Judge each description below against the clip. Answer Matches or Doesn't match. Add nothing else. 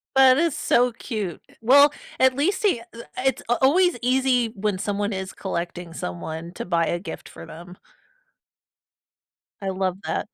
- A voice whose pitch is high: Matches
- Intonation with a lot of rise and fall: Matches